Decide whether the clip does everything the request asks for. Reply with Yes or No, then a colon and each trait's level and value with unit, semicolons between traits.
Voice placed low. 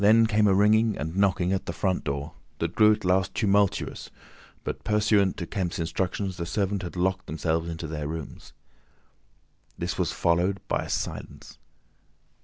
Yes: very low, 95 Hz